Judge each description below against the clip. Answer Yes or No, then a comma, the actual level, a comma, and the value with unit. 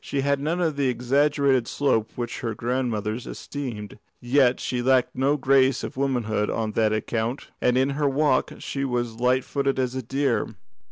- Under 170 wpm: No, average, 175 wpm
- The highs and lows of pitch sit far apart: No, narrow, 2.6 semitones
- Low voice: Yes, low, 130 Hz